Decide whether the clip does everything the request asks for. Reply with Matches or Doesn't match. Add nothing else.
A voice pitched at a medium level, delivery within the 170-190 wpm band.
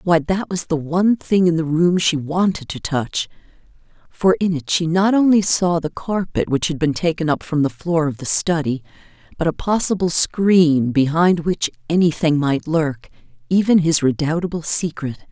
Matches